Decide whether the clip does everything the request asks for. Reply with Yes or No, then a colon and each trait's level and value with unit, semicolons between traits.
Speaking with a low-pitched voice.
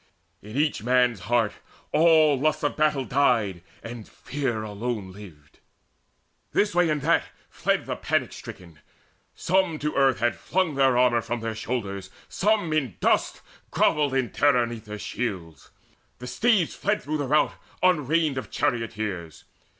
Yes: low, 125 Hz